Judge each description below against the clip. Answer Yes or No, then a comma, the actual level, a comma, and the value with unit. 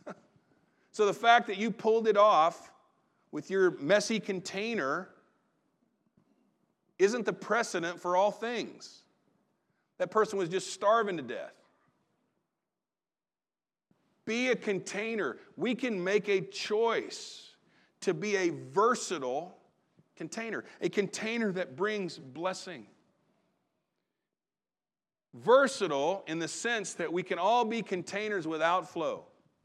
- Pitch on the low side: No, high, 205 Hz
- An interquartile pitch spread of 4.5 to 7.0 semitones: No, average, 3.4 semitones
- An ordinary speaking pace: No, slow, 110 wpm